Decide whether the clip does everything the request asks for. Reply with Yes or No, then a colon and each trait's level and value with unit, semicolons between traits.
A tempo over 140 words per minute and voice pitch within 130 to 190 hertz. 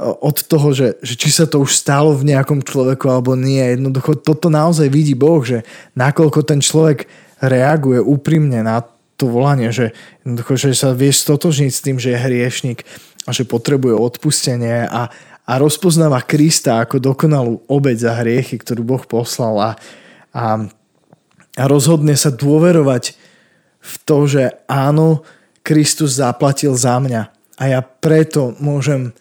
Yes: average, 150 wpm; low, 135 Hz